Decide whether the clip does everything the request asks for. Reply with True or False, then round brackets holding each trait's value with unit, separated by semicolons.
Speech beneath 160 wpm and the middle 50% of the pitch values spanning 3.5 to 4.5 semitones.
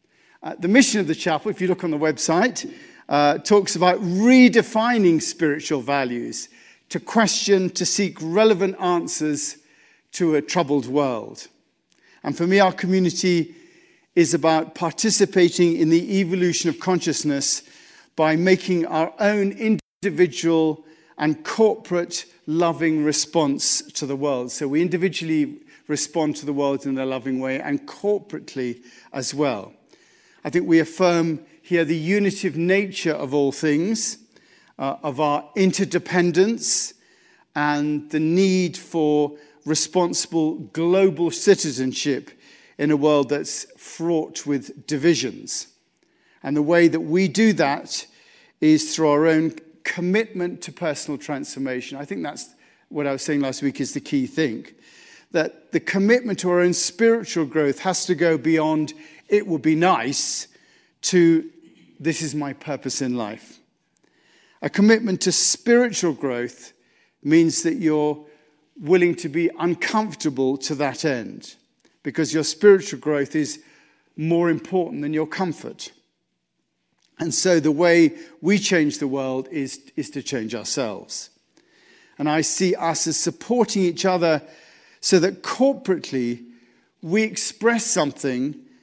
True (135 wpm; 4.0 semitones)